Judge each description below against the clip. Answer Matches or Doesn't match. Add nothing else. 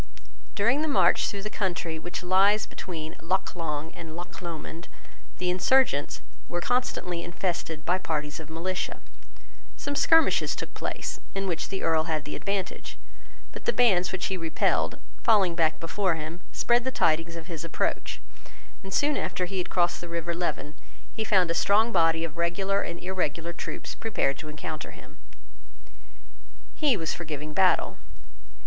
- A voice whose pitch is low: Doesn't match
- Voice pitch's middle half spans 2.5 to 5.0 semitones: Matches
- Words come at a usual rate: Matches